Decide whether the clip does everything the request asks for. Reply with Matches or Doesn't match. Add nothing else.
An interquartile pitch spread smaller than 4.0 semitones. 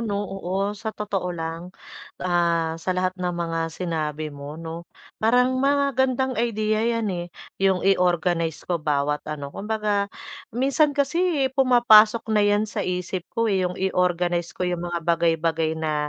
Doesn't match